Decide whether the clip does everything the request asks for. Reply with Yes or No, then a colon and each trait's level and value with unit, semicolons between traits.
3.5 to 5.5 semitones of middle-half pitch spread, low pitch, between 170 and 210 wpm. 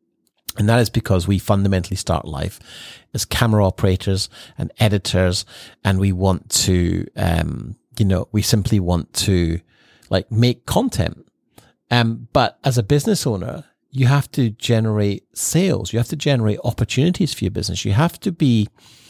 No: average, 4.2 semitones; low, 105 Hz; average, 155 wpm